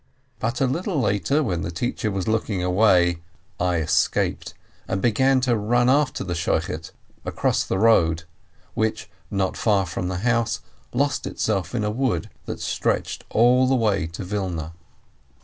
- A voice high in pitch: No, low, 105 Hz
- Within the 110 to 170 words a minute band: Yes, average, 155 wpm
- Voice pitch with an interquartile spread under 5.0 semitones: No, average, 5.3 semitones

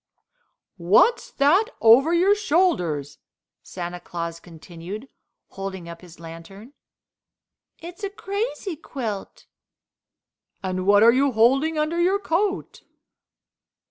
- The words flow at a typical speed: No, slow, 105 wpm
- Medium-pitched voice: No, high, 235 Hz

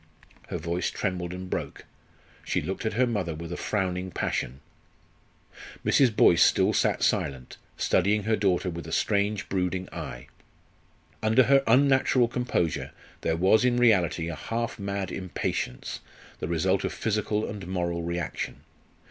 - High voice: No, very low, 95 Hz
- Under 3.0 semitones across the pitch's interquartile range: No, average, 4.1 semitones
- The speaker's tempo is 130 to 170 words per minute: Yes, average, 145 wpm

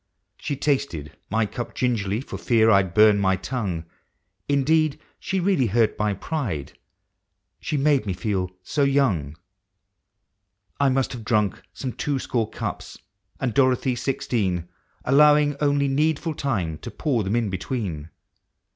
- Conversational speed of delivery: Yes, average, 155 wpm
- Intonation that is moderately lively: No, wide, 6.1 semitones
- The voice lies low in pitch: Yes, low, 120 Hz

